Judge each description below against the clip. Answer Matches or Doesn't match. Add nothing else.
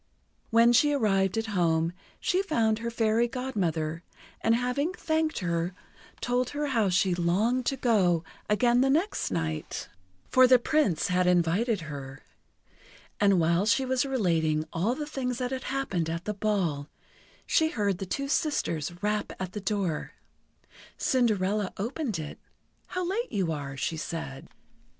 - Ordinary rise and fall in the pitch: Doesn't match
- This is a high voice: Matches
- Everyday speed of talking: Matches